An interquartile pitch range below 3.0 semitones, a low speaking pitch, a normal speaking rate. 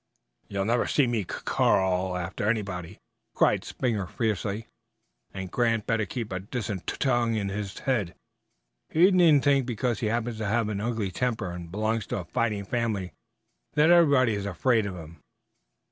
No: average, 3.8 semitones; low, 110 Hz; average, 170 wpm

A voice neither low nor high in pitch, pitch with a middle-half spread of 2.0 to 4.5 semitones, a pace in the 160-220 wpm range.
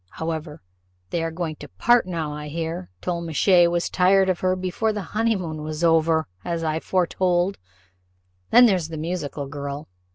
Yes: medium, 170 Hz; average, 2.9 semitones; average, 165 wpm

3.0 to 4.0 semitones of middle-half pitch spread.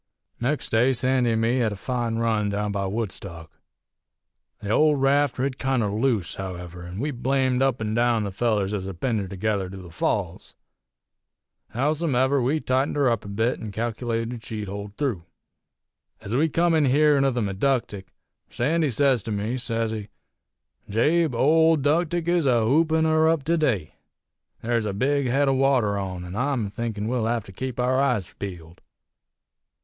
No: average, 5.0 semitones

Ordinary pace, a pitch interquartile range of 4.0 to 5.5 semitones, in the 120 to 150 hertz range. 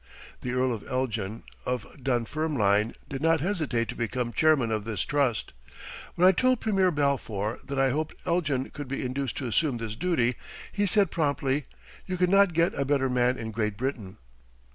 Yes: average, 180 wpm; average, 5.2 semitones; low, 135 Hz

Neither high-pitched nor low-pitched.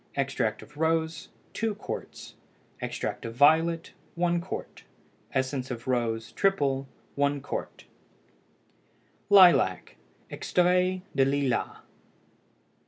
Yes: medium, 145 Hz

